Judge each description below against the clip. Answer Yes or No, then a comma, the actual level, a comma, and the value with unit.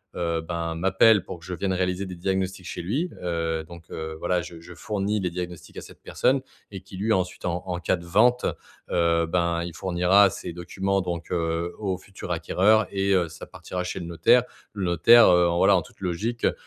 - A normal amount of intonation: No, narrow, 2.2 semitones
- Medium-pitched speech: No, very low, 90 Hz